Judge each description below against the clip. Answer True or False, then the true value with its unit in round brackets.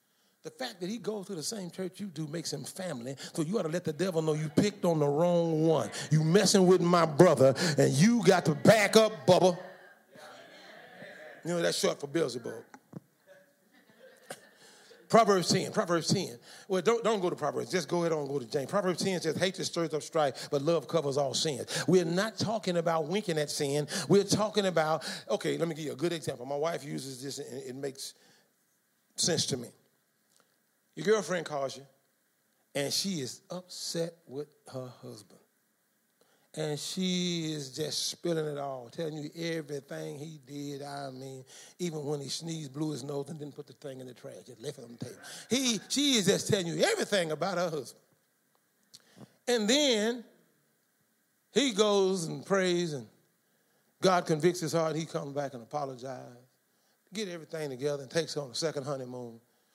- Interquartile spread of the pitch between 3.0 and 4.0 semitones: False (4.5 semitones)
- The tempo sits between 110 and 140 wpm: False (185 wpm)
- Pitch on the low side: False (165 Hz)